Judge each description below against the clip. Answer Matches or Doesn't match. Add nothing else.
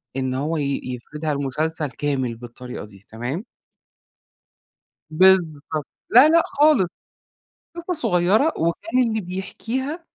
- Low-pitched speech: Doesn't match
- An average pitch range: Doesn't match